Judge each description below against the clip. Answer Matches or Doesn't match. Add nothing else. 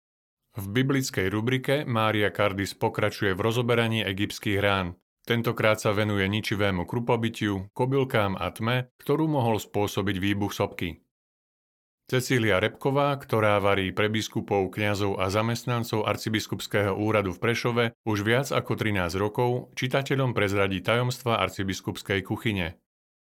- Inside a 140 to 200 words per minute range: Doesn't match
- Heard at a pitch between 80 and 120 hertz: Matches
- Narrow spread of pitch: Doesn't match